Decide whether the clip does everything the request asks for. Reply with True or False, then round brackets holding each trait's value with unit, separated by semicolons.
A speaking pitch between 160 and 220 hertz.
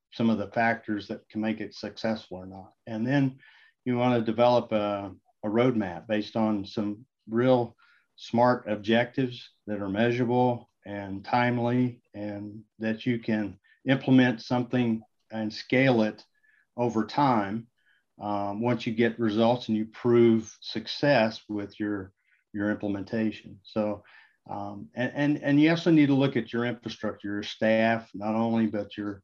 False (110 Hz)